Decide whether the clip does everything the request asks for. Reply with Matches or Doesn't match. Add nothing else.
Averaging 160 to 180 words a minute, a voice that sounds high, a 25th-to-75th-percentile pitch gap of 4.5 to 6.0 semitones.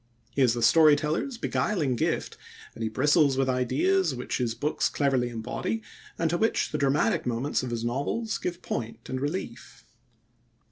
Doesn't match